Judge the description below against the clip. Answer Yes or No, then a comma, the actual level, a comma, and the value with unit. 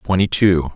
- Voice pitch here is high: No, very low, 85 Hz